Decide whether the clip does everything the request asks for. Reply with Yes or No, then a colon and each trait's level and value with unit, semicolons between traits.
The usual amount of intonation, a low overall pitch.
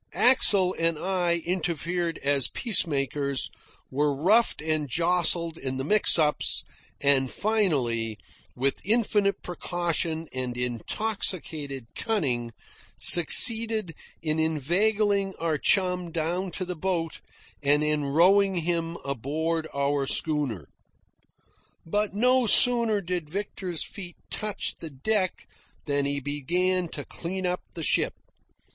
No: average, 4.9 semitones; medium, 165 Hz